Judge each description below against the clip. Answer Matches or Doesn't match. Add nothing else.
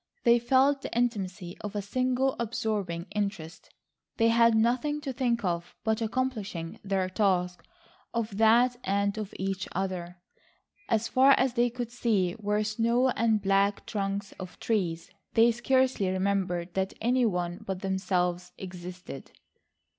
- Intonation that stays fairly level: Doesn't match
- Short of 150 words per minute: Matches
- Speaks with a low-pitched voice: Doesn't match